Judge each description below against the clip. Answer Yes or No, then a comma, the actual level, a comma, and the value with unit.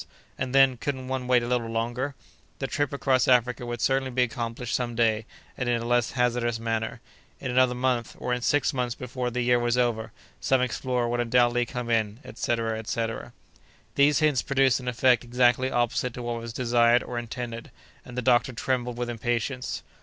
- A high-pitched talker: No, low, 120 Hz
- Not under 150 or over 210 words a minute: Yes, average, 180 wpm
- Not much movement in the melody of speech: Yes, narrow, 1.4 semitones